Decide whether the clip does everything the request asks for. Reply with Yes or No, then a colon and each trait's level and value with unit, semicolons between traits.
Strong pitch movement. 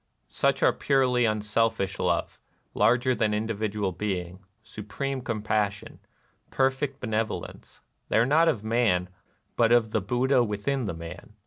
No: average, 3.4 semitones